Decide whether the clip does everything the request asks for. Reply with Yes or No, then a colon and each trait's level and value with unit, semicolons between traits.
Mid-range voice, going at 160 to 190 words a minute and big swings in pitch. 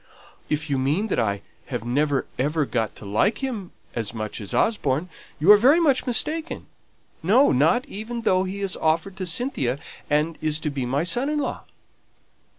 Yes: medium, 165 Hz; average, 175 wpm; wide, 8.7 semitones